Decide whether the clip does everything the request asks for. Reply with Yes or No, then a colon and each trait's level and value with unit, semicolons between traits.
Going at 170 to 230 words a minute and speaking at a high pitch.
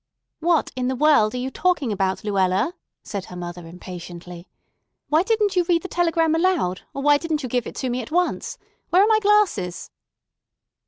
Yes: average, 190 wpm; very high, 265 Hz